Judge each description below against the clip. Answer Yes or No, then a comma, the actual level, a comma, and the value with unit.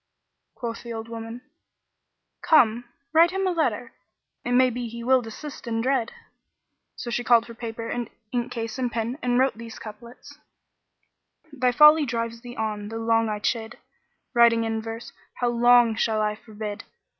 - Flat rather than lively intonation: Yes, narrow, 1.6 semitones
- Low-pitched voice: No, high, 235 Hz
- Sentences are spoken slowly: No, average, 170 wpm